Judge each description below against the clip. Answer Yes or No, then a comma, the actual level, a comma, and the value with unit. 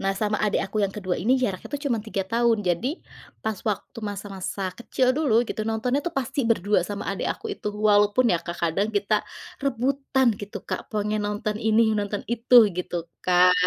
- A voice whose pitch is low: No, high, 210 Hz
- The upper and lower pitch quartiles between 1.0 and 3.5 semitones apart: Yes, average, 3.0 semitones